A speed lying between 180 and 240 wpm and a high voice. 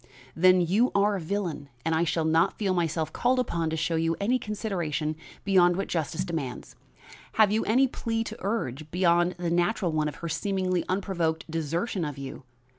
No: average, 185 wpm; medium, 175 Hz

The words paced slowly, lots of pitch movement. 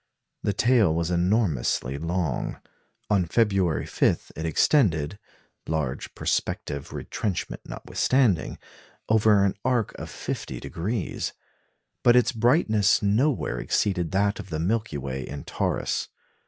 Yes: slow, 115 wpm; wide, 5.7 semitones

